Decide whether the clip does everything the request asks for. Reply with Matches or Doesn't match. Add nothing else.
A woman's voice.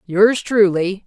Matches